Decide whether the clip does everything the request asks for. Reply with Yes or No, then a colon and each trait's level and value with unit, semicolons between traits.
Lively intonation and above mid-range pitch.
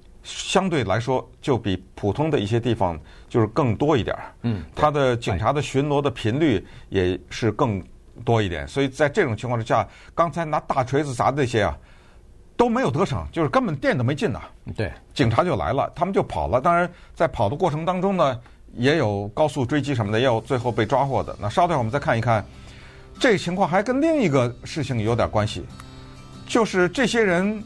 No: wide, 6.8 semitones; low, 125 Hz